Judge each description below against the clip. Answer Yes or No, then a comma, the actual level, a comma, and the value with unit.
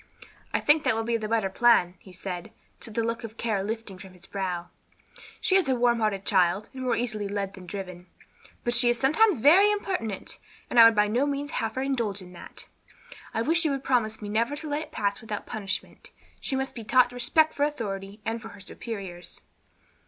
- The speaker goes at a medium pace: No, fast, 210 wpm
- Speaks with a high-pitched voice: Yes, high, 225 Hz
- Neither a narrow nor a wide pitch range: Yes, average, 4.6 semitones